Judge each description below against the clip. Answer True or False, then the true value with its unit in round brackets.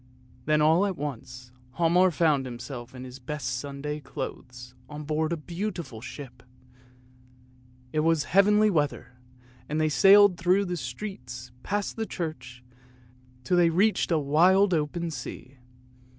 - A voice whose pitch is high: False (150 Hz)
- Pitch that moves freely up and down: True (5.7 semitones)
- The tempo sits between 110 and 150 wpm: True (140 wpm)